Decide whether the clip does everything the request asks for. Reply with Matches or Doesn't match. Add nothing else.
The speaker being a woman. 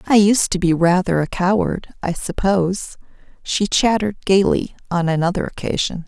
Matches